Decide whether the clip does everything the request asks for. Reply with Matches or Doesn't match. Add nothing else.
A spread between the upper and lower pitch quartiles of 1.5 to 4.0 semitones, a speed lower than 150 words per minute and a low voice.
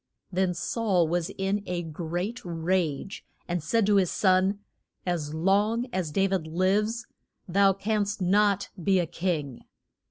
Doesn't match